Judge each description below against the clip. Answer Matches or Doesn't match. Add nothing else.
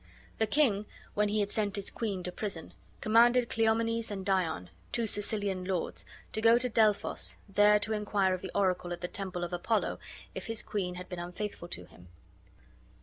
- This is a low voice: Doesn't match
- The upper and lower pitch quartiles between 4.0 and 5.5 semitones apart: Doesn't match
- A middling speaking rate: Matches